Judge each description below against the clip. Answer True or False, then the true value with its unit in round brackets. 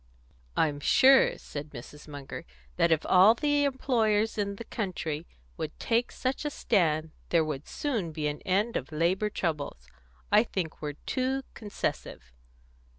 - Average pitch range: False (7.3 semitones)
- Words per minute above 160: False (150 wpm)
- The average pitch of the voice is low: False (185 Hz)